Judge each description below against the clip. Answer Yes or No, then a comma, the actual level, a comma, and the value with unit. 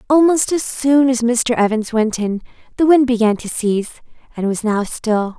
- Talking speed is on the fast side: No, average, 190 wpm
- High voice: Yes, high, 240 Hz